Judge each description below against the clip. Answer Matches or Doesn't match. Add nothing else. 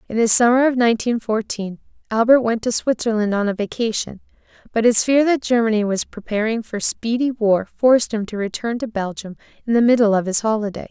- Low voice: Doesn't match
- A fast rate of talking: Doesn't match